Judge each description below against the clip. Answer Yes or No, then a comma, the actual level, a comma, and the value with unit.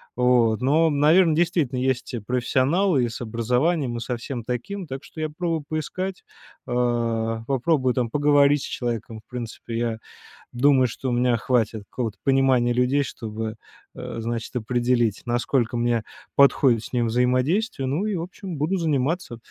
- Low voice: Yes, low, 125 Hz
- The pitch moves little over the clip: No, average, 3.8 semitones